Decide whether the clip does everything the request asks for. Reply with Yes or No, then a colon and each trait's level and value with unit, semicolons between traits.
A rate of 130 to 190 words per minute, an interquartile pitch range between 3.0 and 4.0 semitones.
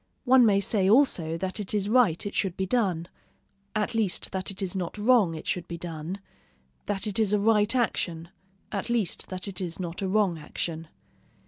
No: average, 200 wpm; average, 3.5 semitones